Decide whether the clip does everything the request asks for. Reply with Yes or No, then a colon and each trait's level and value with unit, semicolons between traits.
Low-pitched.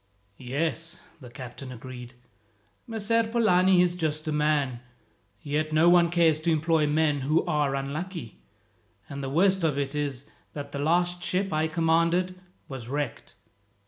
No: medium, 155 Hz